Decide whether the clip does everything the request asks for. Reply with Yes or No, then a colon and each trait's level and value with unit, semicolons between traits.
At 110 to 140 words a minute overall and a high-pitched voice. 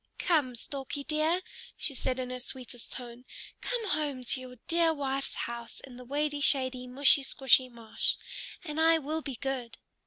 No: average, 165 wpm; very high, 270 Hz